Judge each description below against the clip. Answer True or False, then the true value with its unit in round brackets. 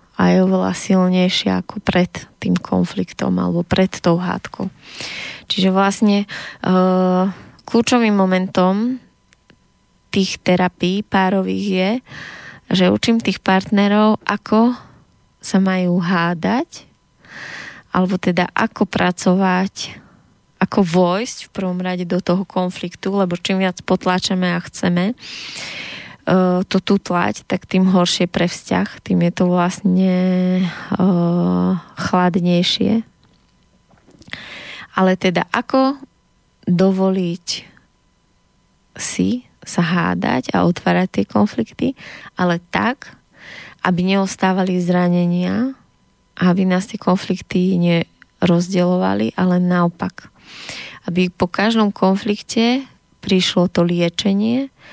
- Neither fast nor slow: False (100 wpm)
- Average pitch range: False (1.8 semitones)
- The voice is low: False (185 Hz)